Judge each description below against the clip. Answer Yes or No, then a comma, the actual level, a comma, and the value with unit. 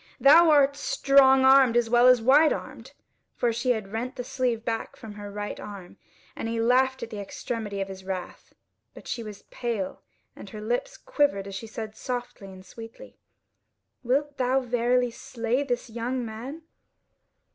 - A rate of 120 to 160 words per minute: No, average, 170 wpm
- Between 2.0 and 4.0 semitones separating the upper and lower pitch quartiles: Yes, average, 3.3 semitones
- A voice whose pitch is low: No, high, 240 Hz